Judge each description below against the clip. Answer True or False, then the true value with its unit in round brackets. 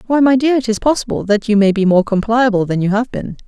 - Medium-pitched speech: False (225 Hz)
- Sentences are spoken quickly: True (275 wpm)